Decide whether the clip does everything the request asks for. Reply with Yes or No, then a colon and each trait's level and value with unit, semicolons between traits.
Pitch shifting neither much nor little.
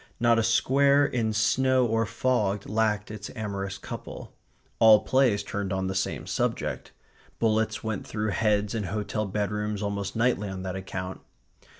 No: narrow, 2.1 semitones